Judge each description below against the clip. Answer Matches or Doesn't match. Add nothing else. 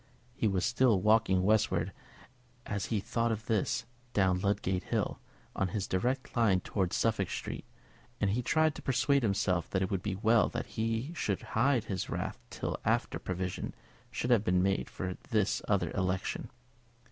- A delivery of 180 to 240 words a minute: Doesn't match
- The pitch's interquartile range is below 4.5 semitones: Matches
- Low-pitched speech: Matches